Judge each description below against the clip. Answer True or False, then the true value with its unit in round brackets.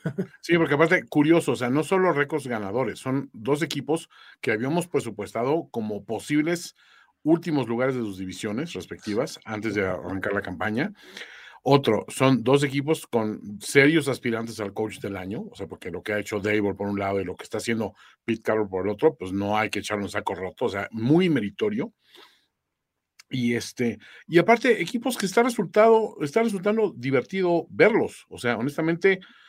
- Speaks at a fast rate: False (180 wpm)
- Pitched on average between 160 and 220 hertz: False (140 Hz)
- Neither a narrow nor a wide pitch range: False (7.9 semitones)